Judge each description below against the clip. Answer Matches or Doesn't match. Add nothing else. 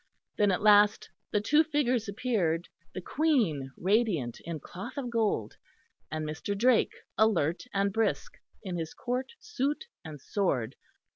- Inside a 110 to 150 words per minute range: Matches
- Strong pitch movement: Matches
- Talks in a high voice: Matches